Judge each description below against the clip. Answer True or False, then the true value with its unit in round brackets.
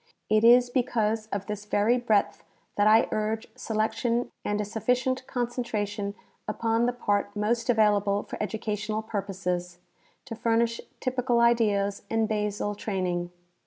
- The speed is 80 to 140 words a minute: True (135 wpm)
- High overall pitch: True (215 Hz)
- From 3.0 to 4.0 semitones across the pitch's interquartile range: False (2.4 semitones)